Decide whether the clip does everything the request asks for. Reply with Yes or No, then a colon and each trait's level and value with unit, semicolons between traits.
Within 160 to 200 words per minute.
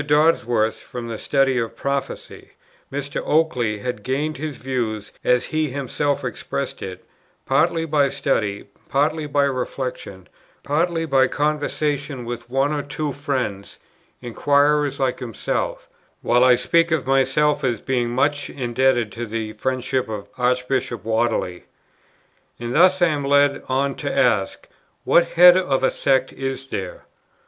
No: average, 140 wpm